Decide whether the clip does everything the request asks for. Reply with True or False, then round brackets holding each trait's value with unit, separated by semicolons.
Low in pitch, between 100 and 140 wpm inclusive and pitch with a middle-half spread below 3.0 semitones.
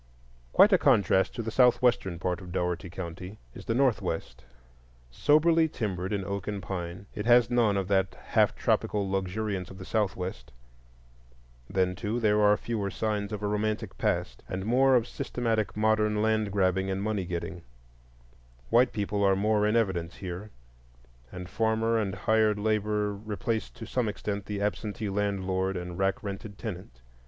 False (105 Hz; 160 wpm; 2.5 semitones)